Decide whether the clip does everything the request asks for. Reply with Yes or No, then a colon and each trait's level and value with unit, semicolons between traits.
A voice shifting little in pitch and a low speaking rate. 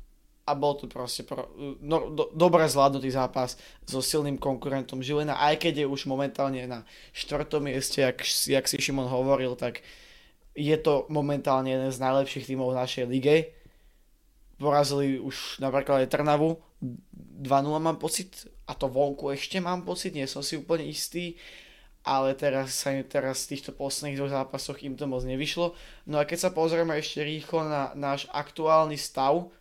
No: narrow, 2.1 semitones; average, 160 wpm